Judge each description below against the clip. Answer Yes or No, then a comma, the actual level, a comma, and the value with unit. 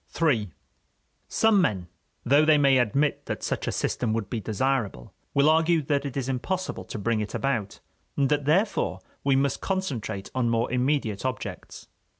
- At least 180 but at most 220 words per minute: No, average, 165 wpm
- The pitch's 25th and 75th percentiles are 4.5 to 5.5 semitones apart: Yes, average, 4.8 semitones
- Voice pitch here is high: No, low, 135 Hz